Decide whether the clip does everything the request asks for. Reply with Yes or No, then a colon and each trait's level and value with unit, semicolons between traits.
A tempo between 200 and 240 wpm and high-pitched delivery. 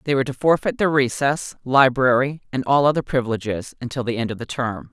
No: fast, 205 wpm; low, 130 Hz